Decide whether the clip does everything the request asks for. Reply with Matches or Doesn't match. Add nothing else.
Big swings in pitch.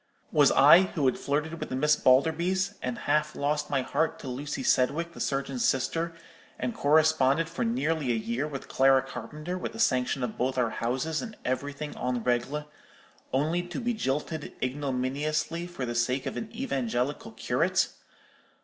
Doesn't match